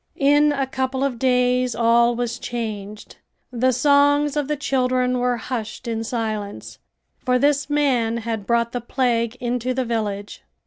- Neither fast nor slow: Yes, average, 150 wpm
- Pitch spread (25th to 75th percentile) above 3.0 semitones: No, narrow, 2.4 semitones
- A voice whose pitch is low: No, very high, 250 Hz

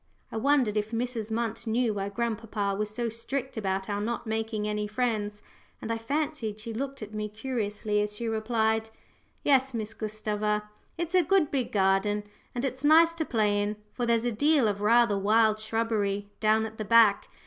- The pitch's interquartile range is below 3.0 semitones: Yes, narrow, 2.4 semitones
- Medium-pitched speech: No, high, 220 Hz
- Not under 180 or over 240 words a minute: Yes, average, 185 wpm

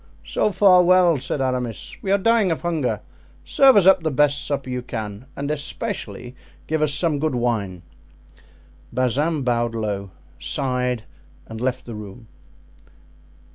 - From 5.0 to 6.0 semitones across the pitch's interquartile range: Yes, average, 5.3 semitones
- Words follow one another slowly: No, average, 145 wpm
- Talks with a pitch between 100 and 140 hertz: Yes, low, 135 Hz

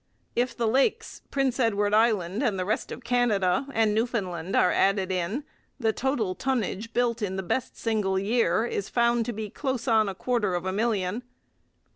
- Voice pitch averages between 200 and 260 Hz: Yes, high, 220 Hz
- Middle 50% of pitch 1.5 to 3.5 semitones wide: No, average, 3.9 semitones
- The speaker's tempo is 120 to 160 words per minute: No, average, 175 wpm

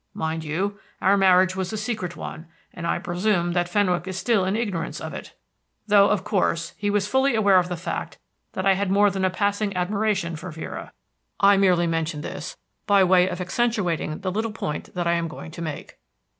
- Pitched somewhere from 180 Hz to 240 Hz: Yes, medium, 185 Hz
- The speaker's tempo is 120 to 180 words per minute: No, fast, 205 wpm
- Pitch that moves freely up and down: No, average, 2.8 semitones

